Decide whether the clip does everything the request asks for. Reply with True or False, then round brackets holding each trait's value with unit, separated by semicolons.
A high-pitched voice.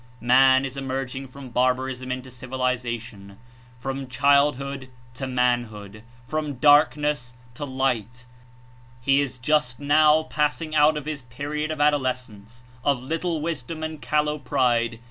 False (135 Hz)